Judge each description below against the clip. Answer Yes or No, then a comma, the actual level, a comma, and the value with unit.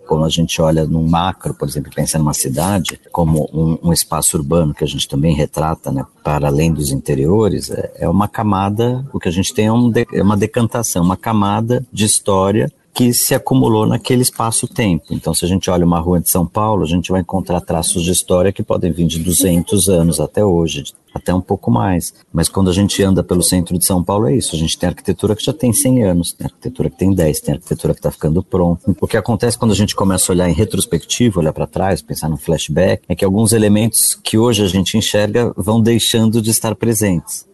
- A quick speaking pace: Yes, fast, 225 wpm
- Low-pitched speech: Yes, very low, 95 Hz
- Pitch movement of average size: Yes, average, 4.5 semitones